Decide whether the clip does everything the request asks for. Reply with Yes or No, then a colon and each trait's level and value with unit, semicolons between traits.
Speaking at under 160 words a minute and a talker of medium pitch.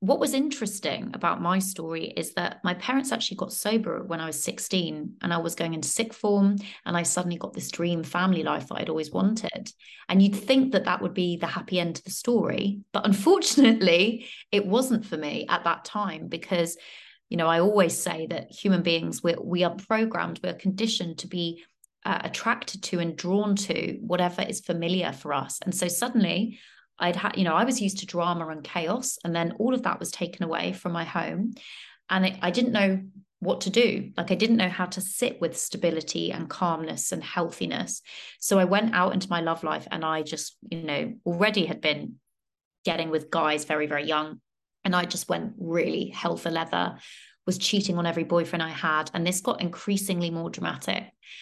No: fast, 205 wpm; medium, 180 Hz